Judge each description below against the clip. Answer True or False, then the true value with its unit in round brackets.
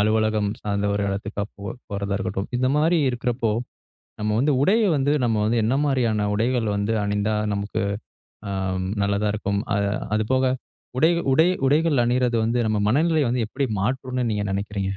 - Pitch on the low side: True (110 Hz)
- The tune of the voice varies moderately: True (4.0 semitones)